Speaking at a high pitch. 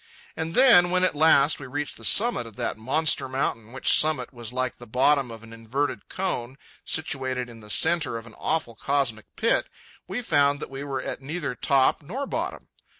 No: medium, 140 Hz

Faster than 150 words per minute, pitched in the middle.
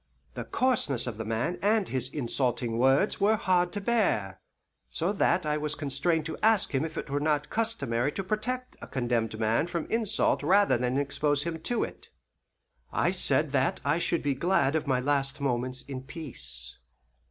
Yes: average, 185 wpm; medium, 145 Hz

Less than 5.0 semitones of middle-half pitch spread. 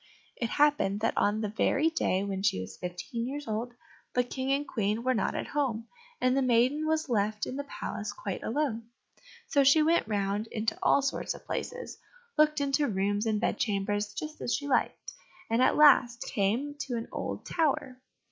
No: average, 5.3 semitones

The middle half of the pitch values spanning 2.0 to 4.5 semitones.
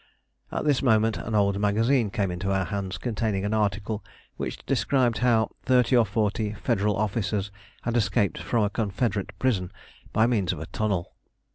Yes: narrow, 2.6 semitones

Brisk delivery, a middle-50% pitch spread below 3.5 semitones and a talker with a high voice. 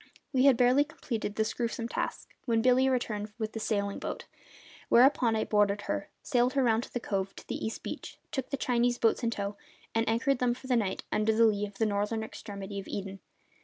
Yes: fast, 215 wpm; average, 3.1 semitones; high, 225 Hz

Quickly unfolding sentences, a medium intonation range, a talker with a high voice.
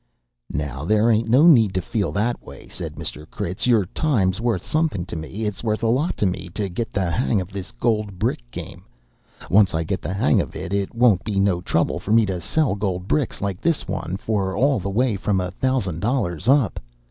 No: fast, 220 wpm; average, 4.1 semitones; low, 100 Hz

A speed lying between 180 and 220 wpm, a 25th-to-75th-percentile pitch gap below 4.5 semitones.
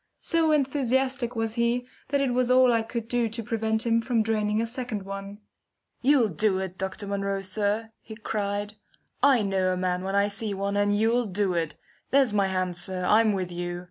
Yes: average, 200 wpm; average, 3.3 semitones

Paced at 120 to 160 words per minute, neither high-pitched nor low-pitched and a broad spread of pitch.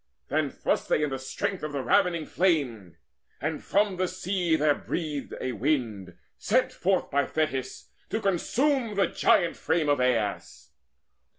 Yes: average, 150 wpm; medium, 155 Hz; wide, 5.7 semitones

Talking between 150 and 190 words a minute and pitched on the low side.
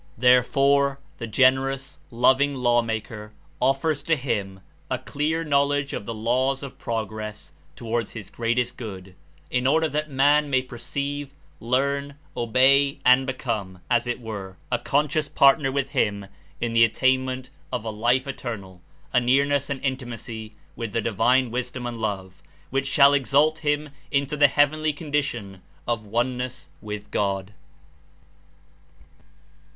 No: average, 140 wpm; low, 130 Hz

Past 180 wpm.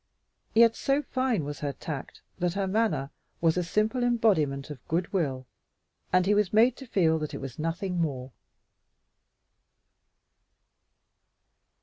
No: slow, 135 wpm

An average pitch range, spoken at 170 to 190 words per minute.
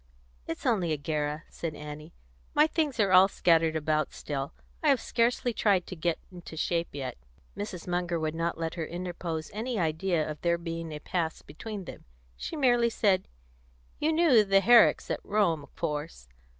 Yes: average, 4.8 semitones; average, 175 wpm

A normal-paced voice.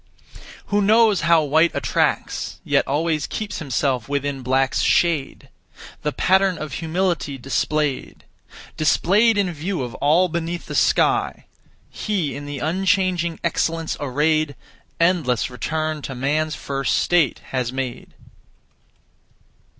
No: slow, 120 wpm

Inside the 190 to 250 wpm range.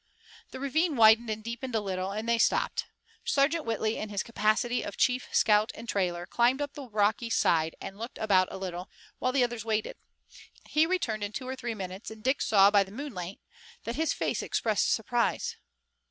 Yes: average, 195 wpm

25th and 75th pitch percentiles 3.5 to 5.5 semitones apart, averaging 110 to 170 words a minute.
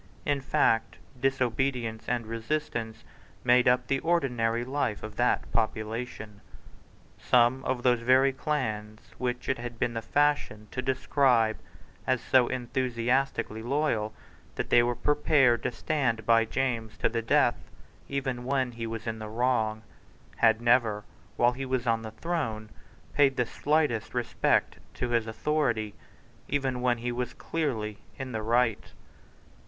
No: average, 2.8 semitones; average, 145 wpm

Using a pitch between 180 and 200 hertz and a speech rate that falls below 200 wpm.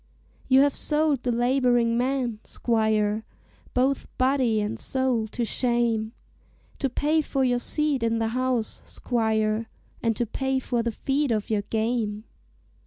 No: high, 240 Hz; average, 145 wpm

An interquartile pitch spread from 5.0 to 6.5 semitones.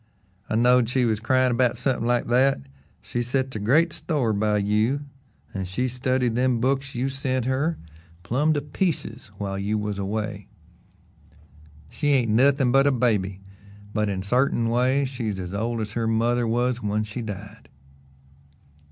No: average, 3.5 semitones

